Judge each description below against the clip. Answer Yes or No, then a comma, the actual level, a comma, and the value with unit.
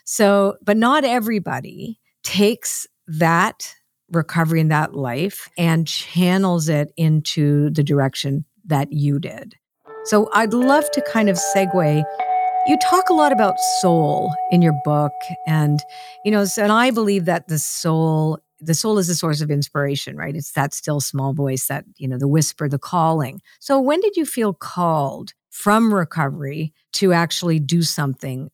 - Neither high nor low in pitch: Yes, medium, 170 Hz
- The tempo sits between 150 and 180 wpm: Yes, average, 160 wpm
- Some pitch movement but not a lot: No, wide, 5.8 semitones